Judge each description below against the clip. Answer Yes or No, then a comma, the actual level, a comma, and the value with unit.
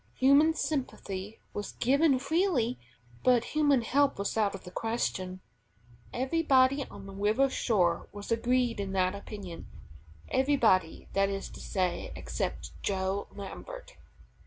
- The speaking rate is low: Yes, slow, 130 wpm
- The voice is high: Yes, high, 230 Hz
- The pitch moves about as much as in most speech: No, wide, 5.7 semitones